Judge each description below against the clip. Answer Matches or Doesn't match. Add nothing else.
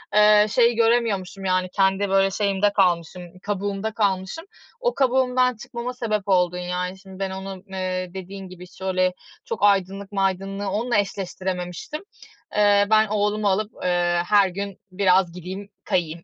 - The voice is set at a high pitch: Matches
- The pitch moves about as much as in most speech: Doesn't match